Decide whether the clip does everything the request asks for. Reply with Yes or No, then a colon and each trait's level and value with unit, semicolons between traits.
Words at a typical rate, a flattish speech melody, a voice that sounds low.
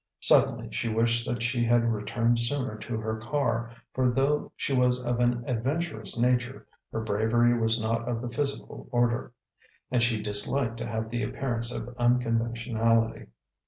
Yes: average, 160 wpm; narrow, 1.4 semitones; low, 120 Hz